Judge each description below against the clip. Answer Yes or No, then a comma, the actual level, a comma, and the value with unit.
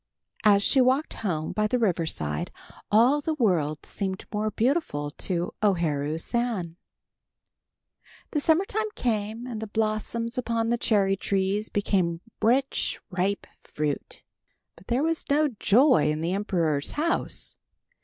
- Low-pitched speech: No, high, 210 Hz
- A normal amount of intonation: No, wide, 6.0 semitones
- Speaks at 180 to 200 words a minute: No, average, 140 wpm